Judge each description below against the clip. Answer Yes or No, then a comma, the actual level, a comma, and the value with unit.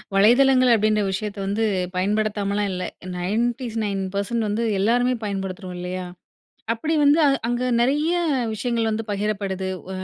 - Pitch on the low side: No, high, 215 Hz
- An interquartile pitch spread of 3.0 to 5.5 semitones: Yes, average, 3.3 semitones